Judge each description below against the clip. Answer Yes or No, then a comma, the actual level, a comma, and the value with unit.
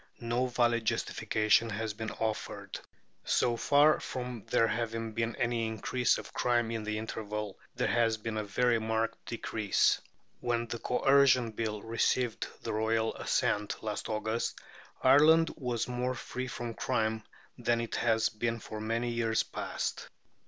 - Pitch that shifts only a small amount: Yes, narrow, 1.5 semitones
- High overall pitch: No, low, 115 Hz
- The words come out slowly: No, average, 145 wpm